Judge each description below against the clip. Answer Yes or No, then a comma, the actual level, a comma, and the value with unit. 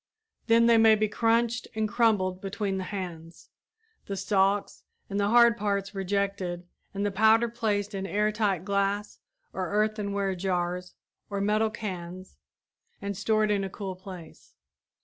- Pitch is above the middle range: Yes, high, 200 Hz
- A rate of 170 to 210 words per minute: No, average, 150 wpm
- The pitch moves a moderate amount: No, narrow, 2.1 semitones